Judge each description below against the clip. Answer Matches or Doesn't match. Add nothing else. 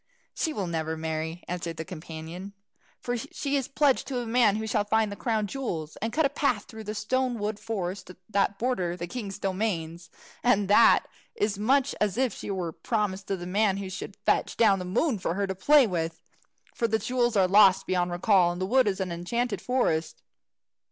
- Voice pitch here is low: Doesn't match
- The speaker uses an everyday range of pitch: Matches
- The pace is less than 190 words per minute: Doesn't match